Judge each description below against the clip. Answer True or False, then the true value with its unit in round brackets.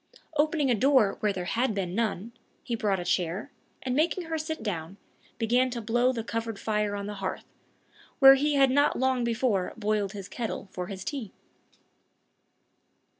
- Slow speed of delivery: False (170 wpm)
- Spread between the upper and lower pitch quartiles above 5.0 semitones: False (4.6 semitones)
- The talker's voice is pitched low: False (225 Hz)